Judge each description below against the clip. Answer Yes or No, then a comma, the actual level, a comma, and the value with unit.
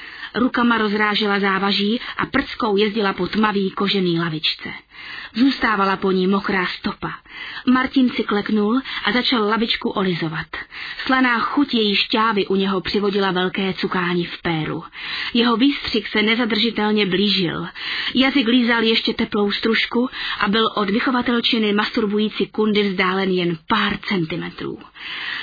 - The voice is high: Yes, high, 215 Hz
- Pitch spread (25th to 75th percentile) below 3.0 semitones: No, average, 3.3 semitones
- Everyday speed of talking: Yes, average, 125 wpm